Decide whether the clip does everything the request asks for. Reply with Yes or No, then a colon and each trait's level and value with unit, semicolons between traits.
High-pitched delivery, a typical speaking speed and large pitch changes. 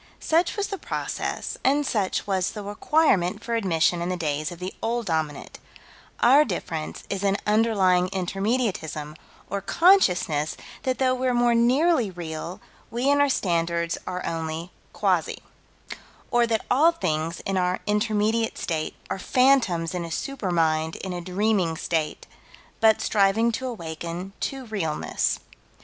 Yes: high, 195 Hz; average, 145 wpm; wide, 6.0 semitones